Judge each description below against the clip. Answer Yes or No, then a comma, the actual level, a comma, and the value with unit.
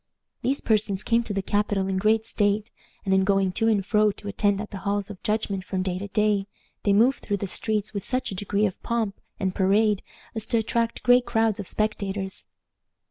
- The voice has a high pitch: Yes, high, 205 Hz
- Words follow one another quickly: Yes, fast, 210 wpm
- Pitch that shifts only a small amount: Yes, narrow, 2.0 semitones